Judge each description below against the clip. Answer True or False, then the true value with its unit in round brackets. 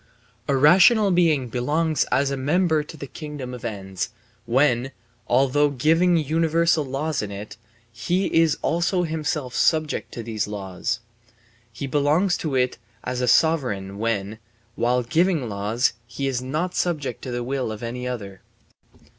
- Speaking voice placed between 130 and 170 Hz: True (135 Hz)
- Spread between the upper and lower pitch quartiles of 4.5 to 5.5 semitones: True (5.0 semitones)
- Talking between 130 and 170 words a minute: True (145 wpm)